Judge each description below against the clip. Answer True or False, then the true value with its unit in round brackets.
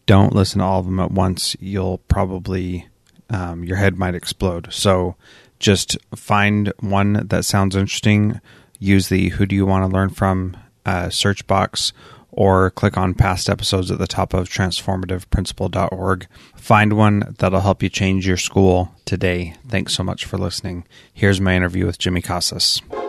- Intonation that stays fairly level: True (1.6 semitones)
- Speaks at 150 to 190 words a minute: True (165 wpm)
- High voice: False (95 Hz)